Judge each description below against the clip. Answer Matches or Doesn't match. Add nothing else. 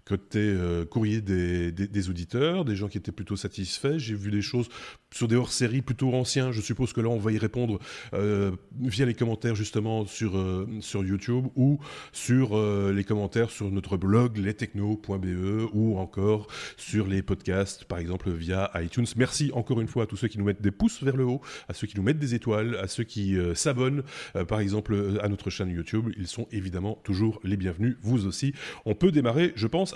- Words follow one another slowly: Doesn't match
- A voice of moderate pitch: Doesn't match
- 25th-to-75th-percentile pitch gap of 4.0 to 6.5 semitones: Doesn't match